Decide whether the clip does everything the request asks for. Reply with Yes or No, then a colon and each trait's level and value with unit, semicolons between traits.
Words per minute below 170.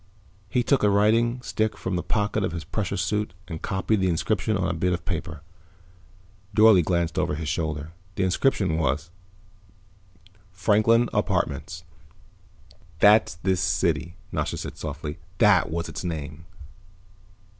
Yes: average, 140 wpm